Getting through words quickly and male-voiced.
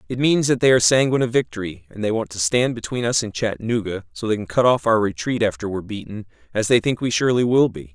Yes: fast, 255 wpm; male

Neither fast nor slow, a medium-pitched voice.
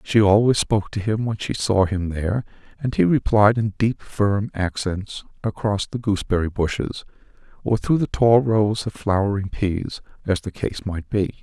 No: average, 180 wpm; low, 105 Hz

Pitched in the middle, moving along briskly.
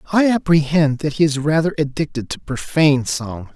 No: medium, 150 Hz; average, 170 wpm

